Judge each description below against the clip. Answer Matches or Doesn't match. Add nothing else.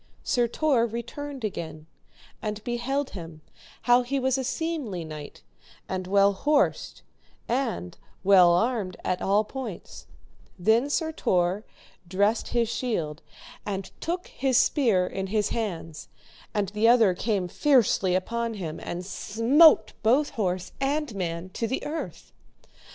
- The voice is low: Doesn't match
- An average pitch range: Doesn't match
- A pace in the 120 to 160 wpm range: Matches